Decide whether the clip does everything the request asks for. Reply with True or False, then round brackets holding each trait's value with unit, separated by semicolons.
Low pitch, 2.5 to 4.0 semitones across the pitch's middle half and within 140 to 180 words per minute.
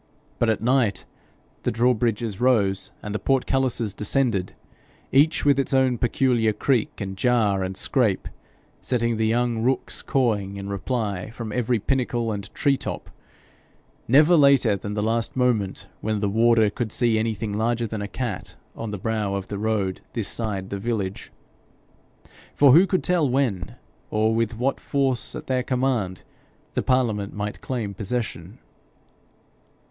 True (115 Hz; 3.7 semitones; 150 wpm)